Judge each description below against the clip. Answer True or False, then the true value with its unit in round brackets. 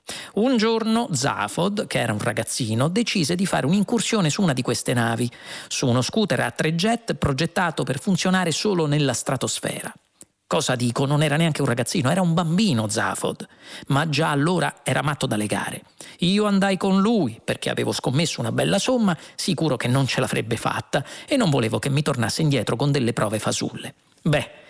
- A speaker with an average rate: False (180 wpm)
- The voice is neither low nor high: True (155 Hz)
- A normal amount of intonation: False (6.8 semitones)